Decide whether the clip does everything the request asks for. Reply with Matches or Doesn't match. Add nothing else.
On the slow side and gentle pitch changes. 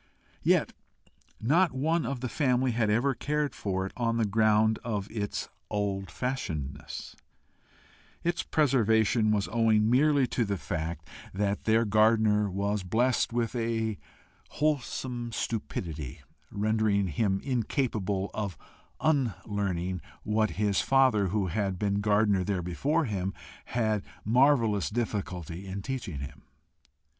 Doesn't match